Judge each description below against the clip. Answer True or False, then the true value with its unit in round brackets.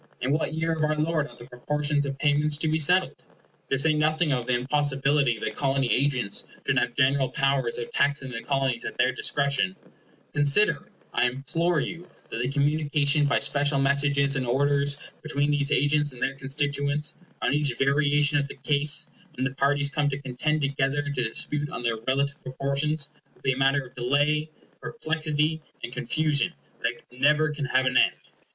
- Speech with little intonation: True (1.9 semitones)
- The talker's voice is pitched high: False (140 Hz)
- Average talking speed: True (185 wpm)